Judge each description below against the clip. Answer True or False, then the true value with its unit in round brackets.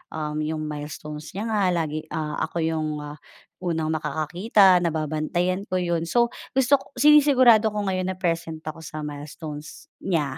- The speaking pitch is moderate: True (160 Hz)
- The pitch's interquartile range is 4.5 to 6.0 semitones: False (3.6 semitones)